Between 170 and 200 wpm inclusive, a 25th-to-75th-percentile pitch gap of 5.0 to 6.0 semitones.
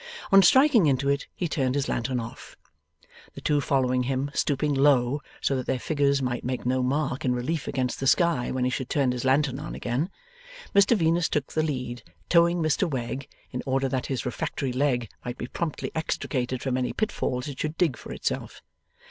No: average, 195 wpm; average, 3.3 semitones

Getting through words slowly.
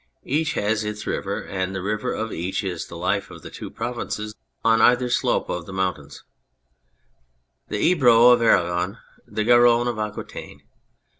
No: average, 160 wpm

